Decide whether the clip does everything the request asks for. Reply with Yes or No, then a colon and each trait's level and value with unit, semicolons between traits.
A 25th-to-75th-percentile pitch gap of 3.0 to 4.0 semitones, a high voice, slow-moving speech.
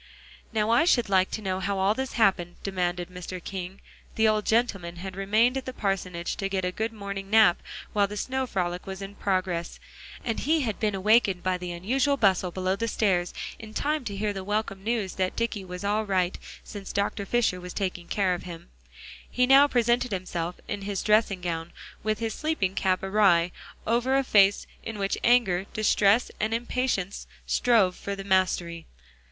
No: average, 3.3 semitones; high, 200 Hz; average, 185 wpm